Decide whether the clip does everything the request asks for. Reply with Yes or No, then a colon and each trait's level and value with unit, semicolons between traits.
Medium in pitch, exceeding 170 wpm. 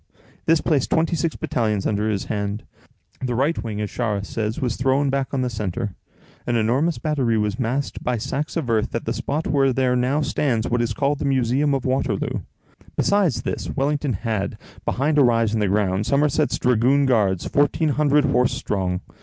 No: low, 125 Hz; average, 185 wpm